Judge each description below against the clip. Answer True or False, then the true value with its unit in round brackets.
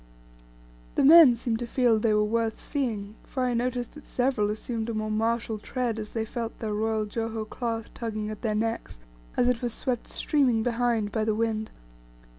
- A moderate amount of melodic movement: False (2.0 semitones)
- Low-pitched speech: False (225 Hz)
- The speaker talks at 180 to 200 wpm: True (190 wpm)